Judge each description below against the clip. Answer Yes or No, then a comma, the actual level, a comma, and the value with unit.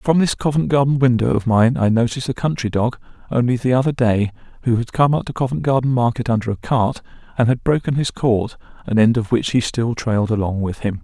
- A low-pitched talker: Yes, low, 120 Hz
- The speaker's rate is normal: No, fast, 230 wpm